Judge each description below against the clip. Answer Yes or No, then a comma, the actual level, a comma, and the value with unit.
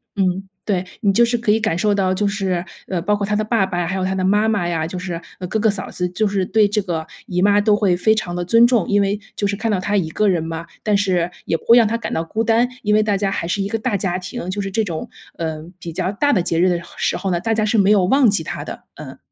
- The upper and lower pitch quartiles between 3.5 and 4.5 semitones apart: No, average, 3.0 semitones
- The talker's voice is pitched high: Yes, high, 200 Hz